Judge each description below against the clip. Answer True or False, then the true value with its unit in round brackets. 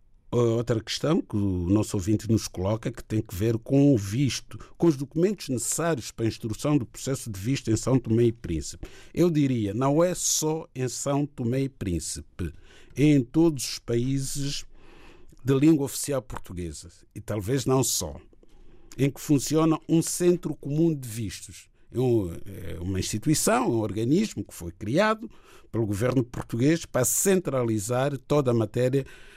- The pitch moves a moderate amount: True (4.8 semitones)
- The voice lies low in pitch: True (120 Hz)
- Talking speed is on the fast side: False (155 wpm)